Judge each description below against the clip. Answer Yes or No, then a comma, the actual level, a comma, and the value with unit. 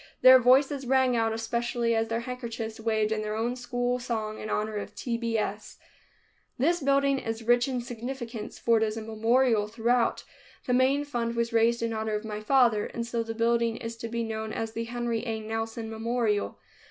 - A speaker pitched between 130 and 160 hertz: No, high, 230 Hz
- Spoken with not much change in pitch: Yes, narrow, 1.7 semitones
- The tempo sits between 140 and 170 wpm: No, average, 200 wpm